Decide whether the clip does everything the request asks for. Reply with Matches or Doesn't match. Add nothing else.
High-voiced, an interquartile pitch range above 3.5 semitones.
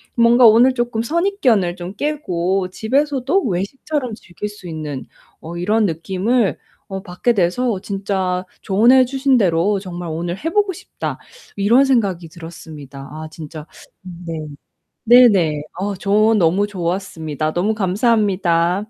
Matches